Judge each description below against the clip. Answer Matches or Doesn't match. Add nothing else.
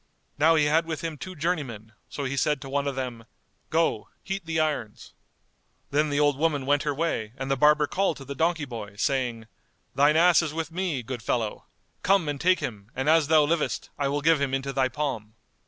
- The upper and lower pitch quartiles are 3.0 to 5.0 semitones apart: Matches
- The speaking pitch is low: Doesn't match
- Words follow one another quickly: Matches